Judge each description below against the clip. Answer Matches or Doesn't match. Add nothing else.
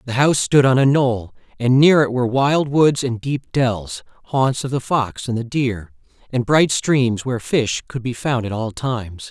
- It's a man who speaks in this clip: Matches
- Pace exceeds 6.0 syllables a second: Doesn't match